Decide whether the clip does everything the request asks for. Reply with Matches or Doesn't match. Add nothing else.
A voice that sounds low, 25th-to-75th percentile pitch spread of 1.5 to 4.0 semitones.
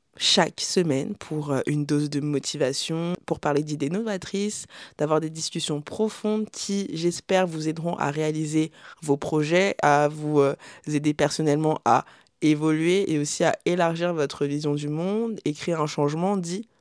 Doesn't match